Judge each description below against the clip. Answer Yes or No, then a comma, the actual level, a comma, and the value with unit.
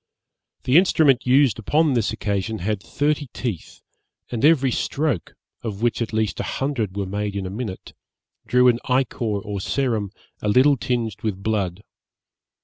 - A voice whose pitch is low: Yes, low, 115 Hz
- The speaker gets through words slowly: No, average, 155 wpm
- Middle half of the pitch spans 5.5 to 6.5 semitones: No, average, 4.5 semitones